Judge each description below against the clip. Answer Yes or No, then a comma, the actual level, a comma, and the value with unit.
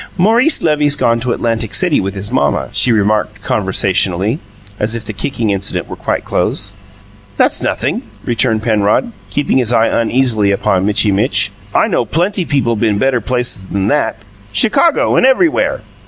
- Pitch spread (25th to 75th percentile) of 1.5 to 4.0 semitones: No, wide, 5.4 semitones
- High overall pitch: No, low, 115 Hz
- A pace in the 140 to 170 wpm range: Yes, average, 160 wpm